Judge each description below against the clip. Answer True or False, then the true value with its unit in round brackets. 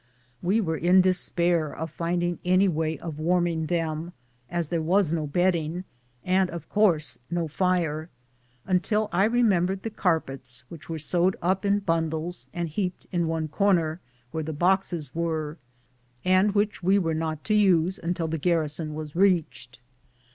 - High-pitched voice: False (170 Hz)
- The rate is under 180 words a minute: True (160 wpm)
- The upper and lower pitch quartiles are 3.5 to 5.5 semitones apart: False (2.7 semitones)